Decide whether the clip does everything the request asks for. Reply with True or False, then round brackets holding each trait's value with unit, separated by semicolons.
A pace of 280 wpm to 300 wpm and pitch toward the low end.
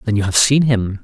True (290 wpm; 110 Hz)